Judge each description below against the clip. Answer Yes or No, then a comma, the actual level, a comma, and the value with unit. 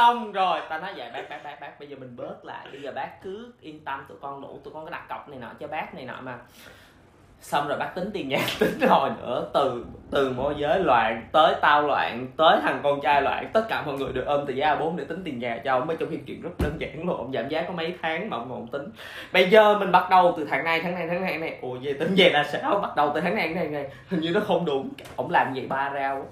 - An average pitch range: Yes, average, 4.4 semitones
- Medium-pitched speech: Yes, medium, 155 Hz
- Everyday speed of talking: No, fast, 300 wpm